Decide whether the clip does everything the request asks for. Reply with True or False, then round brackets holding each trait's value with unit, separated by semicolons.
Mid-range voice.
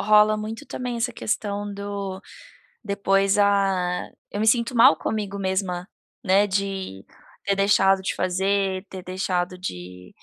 False (195 Hz)